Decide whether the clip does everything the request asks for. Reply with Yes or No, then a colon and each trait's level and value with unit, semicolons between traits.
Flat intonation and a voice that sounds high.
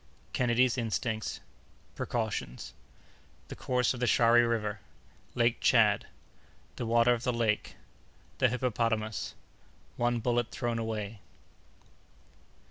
No: narrow, 2.0 semitones; low, 115 Hz